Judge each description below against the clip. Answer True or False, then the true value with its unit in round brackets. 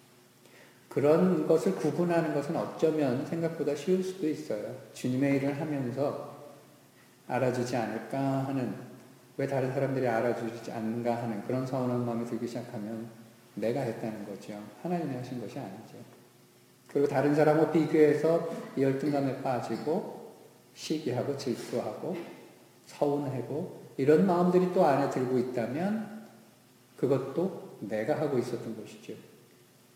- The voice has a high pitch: False (130 Hz)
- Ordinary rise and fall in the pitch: True (3.9 semitones)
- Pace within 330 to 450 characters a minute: False (295 characters per minute)